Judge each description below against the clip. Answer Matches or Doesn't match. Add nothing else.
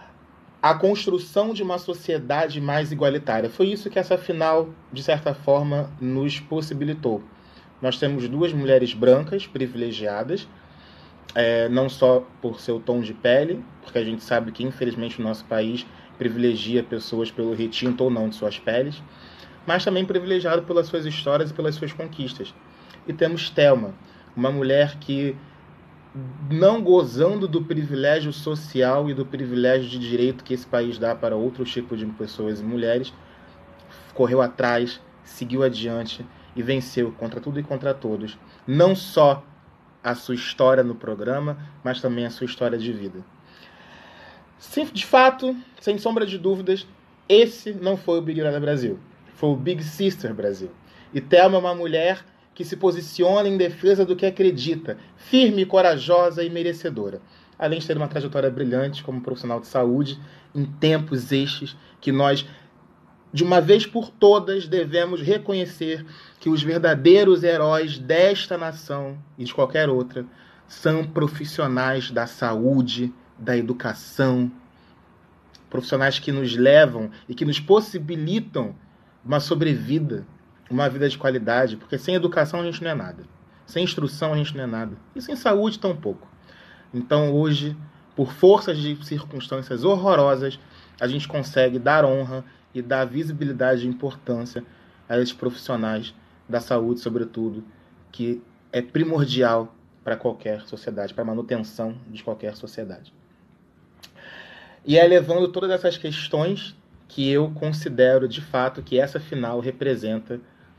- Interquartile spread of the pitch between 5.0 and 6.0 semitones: Matches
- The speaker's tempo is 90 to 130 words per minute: Doesn't match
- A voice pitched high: Doesn't match